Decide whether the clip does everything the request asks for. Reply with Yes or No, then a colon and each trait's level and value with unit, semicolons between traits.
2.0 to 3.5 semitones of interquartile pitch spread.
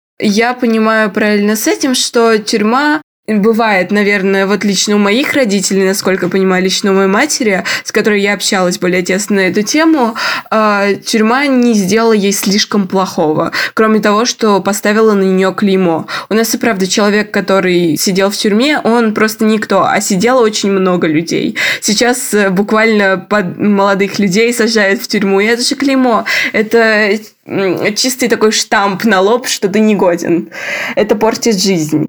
Yes: average, 2.7 semitones